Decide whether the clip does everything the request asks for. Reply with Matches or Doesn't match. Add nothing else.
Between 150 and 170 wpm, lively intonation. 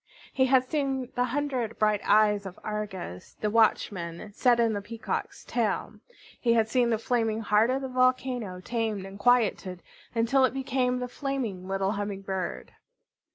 Doesn't match